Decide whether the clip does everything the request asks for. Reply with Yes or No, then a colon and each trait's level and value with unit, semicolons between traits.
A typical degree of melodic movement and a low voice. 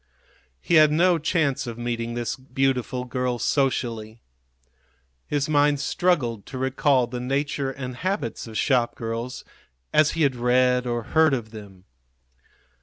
Yes: average, 3.3 semitones; low, 125 Hz